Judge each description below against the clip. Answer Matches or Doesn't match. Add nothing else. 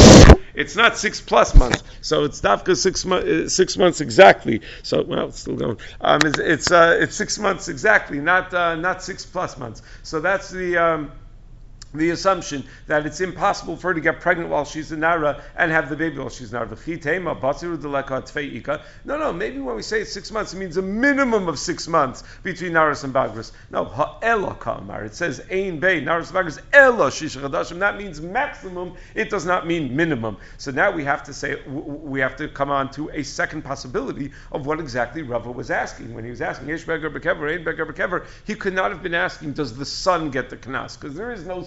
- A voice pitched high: Doesn't match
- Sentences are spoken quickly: Doesn't match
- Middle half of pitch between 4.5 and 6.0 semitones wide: Matches